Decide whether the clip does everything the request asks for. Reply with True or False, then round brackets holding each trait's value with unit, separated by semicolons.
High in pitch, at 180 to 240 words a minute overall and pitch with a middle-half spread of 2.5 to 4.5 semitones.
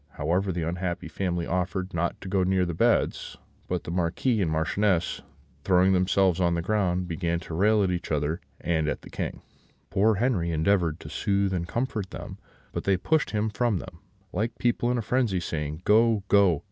False (90 Hz; 190 wpm; 3.2 semitones)